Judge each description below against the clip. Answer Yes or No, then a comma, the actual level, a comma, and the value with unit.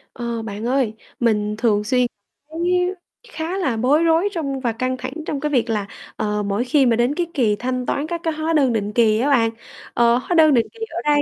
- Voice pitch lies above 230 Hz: Yes, very high, 255 Hz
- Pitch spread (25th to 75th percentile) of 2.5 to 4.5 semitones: No, average, 5.2 semitones